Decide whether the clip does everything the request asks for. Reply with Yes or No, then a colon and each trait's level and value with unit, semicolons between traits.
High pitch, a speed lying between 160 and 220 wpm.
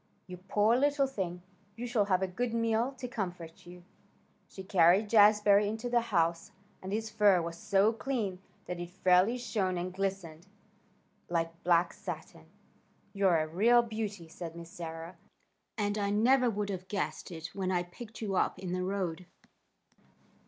Yes: high, 195 Hz; average, 165 wpm